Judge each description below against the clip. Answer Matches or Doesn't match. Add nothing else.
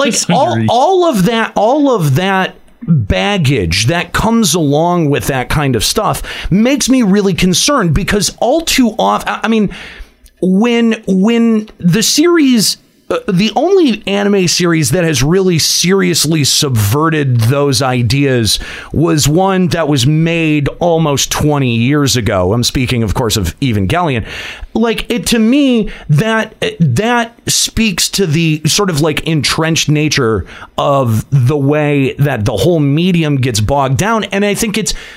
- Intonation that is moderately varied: Doesn't match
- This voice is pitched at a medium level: Matches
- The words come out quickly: Doesn't match